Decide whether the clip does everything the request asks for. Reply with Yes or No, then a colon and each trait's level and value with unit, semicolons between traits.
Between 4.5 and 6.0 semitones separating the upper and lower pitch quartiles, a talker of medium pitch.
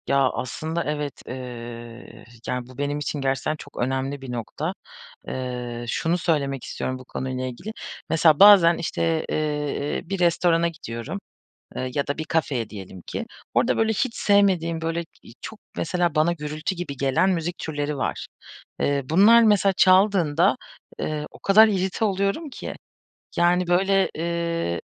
Yes: average, 5.1 semitones; medium, 155 Hz